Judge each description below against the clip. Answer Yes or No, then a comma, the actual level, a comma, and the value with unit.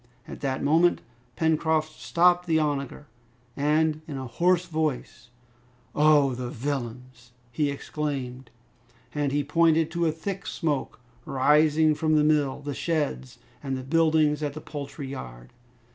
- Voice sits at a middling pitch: Yes, medium, 150 Hz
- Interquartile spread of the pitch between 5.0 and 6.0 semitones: No, average, 2.9 semitones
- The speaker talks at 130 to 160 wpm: Yes, average, 140 wpm